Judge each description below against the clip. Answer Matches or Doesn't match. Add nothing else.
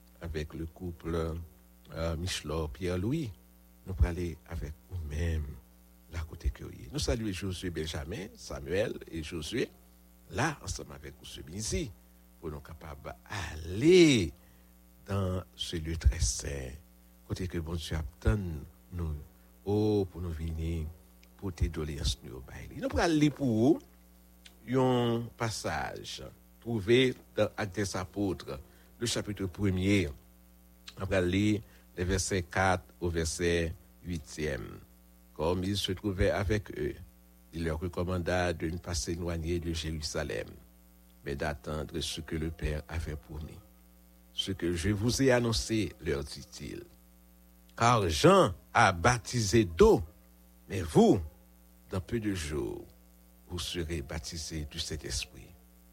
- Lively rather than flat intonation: Matches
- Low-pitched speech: Matches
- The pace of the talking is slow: Matches